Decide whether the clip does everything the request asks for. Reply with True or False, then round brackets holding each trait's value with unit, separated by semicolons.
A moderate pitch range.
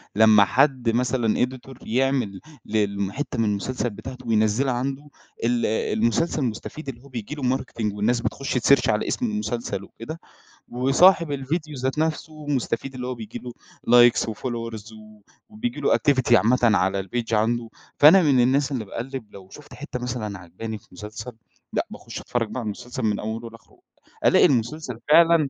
True (3.7 semitones)